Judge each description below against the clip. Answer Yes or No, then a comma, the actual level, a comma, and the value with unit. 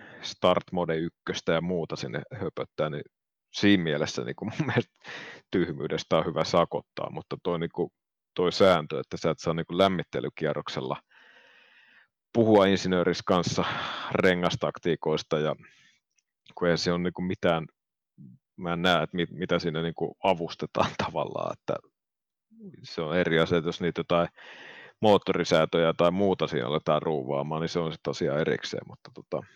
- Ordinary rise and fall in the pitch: No, narrow, 1.9 semitones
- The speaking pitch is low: Yes, very low, 85 Hz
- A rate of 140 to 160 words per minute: Yes, average, 150 wpm